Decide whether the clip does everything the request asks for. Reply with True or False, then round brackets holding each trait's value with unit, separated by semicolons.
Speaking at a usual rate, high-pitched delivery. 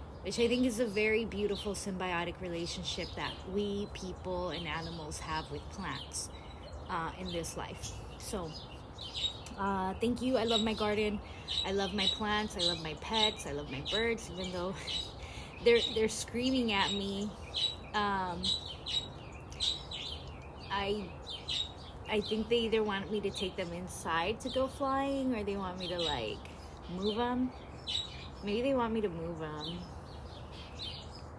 True (150 wpm; 195 Hz)